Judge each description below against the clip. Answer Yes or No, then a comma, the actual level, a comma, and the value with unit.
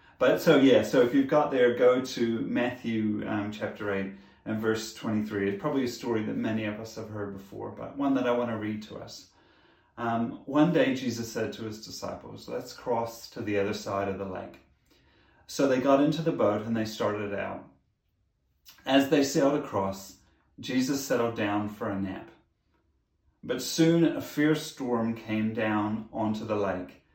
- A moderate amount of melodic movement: Yes, average, 3.7 semitones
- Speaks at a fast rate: No, average, 185 wpm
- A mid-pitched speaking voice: No, low, 110 Hz